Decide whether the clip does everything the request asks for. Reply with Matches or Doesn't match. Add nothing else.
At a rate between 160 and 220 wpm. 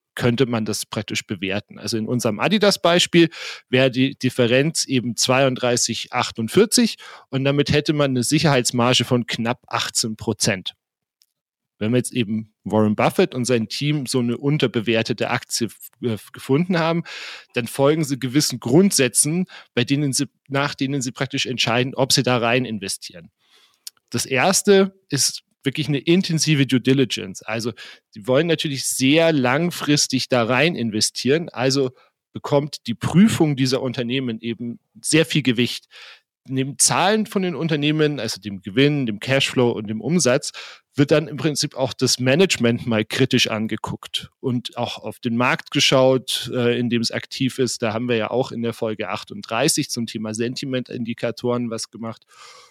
Doesn't match